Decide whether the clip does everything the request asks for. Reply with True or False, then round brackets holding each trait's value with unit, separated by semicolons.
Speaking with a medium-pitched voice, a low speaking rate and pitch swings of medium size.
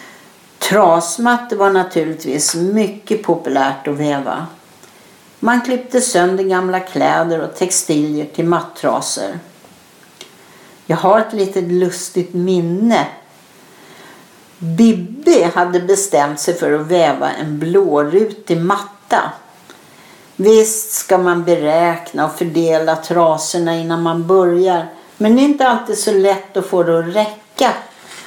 True (180 Hz; 115 wpm; 3.8 semitones)